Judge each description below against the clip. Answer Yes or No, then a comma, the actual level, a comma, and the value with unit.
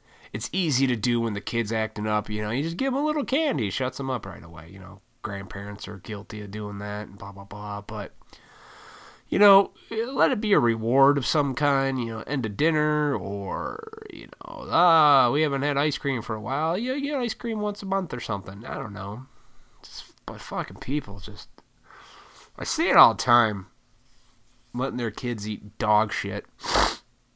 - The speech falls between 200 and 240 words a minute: Yes, fast, 205 wpm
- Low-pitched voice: Yes, low, 120 Hz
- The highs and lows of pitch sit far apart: Yes, wide, 5.9 semitones